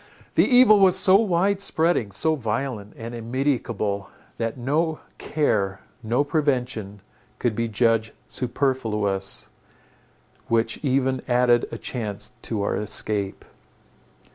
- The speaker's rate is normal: No, slow, 115 wpm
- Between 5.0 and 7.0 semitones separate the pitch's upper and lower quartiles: Yes, average, 5.3 semitones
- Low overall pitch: Yes, low, 120 Hz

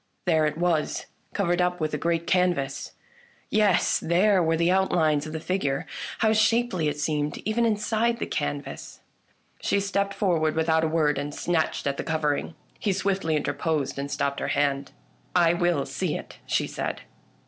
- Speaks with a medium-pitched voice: Yes, medium, 165 Hz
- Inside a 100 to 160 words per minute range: No, average, 170 wpm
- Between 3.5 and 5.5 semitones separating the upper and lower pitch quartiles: Yes, average, 4.1 semitones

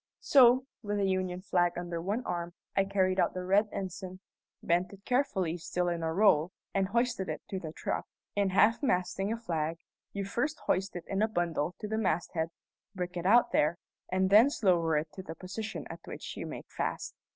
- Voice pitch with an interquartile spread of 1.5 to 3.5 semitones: Yes, average, 2.9 semitones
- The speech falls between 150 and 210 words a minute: Yes, average, 200 wpm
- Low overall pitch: No, medium, 185 Hz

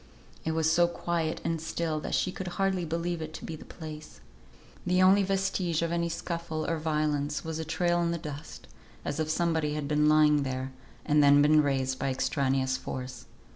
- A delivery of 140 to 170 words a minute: No, average, 195 wpm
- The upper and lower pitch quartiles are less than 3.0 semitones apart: Yes, narrow, 2.4 semitones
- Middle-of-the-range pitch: Yes, medium, 160 Hz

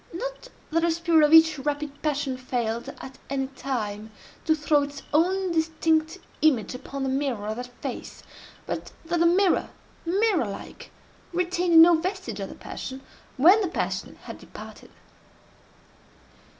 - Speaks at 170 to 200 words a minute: No, average, 145 wpm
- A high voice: Yes, very high, 310 Hz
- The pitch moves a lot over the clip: No, average, 4.3 semitones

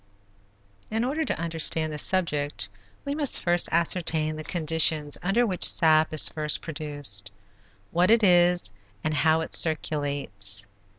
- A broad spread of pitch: No, average, 2.9 semitones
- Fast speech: No, slow, 135 wpm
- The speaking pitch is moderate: Yes, medium, 160 Hz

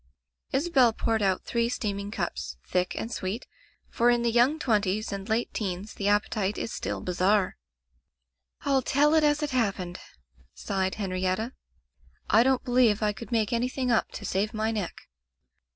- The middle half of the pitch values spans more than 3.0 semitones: Yes, average, 3.6 semitones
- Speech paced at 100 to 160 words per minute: No, average, 170 wpm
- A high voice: Yes, high, 220 Hz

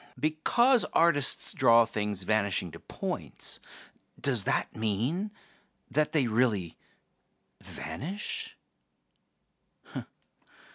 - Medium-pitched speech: No, low, 120 Hz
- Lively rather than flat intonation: Yes, wide, 7.0 semitones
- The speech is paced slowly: Yes, slow, 80 wpm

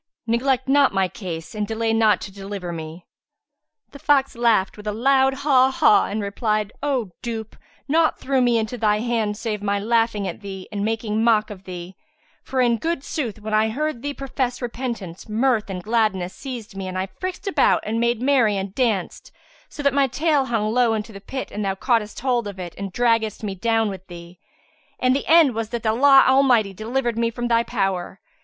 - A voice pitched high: Yes, high, 225 Hz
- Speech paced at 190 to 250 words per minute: Yes, average, 200 wpm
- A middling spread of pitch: Yes, average, 4.0 semitones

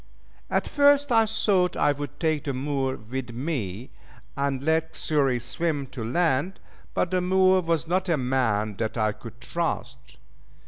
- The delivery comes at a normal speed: Yes, average, 155 wpm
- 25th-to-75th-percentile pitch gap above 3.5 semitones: Yes, wide, 5.4 semitones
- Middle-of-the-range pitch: Yes, medium, 145 Hz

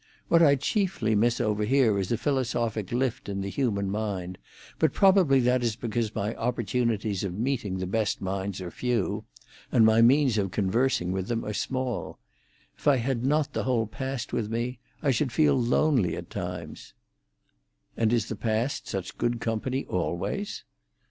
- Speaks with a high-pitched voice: No, low, 115 Hz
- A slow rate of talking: No, average, 170 wpm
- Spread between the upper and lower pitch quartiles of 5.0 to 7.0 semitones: No, average, 4.2 semitones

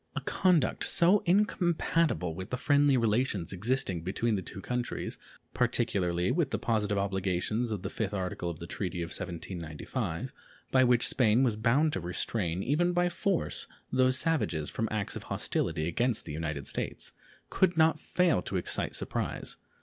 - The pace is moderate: Yes, average, 160 wpm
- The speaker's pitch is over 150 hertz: No, low, 110 Hz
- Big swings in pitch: Yes, wide, 8.0 semitones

